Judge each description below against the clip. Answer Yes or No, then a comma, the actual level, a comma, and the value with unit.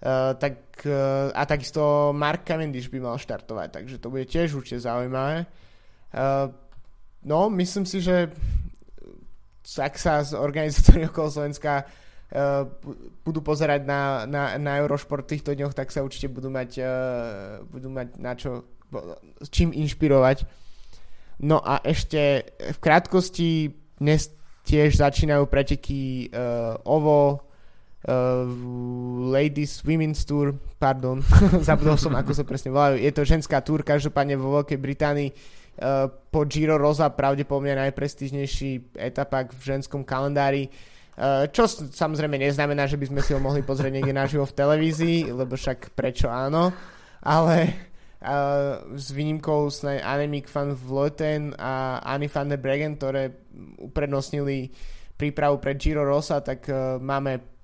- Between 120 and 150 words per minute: Yes, average, 135 wpm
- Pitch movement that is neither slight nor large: No, narrow, 2.1 semitones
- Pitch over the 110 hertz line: Yes, medium, 140 Hz